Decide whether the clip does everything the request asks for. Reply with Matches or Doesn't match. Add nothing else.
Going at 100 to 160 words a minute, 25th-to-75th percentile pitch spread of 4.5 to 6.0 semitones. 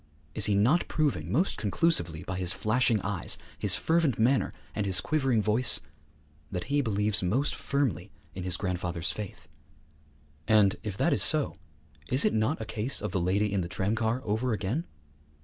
Doesn't match